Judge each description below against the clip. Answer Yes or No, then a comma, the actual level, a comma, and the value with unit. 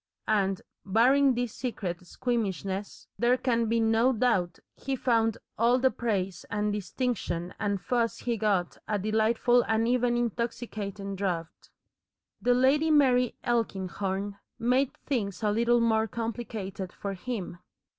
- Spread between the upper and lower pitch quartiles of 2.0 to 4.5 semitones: Yes, average, 3.5 semitones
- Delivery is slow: Yes, slow, 130 wpm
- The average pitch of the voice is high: Yes, high, 225 Hz